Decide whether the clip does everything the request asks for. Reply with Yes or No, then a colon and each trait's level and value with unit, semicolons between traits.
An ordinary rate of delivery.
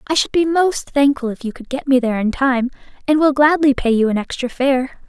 No: fast, 250 wpm